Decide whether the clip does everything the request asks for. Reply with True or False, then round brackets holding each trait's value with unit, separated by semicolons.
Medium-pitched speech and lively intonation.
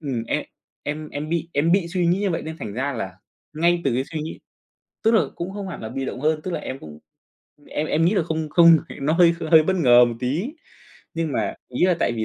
False (155 Hz; 4.2 semitones)